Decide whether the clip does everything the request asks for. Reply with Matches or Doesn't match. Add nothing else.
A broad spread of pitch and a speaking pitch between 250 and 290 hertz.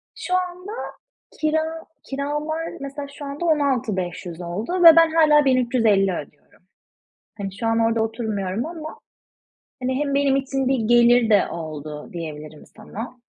Matches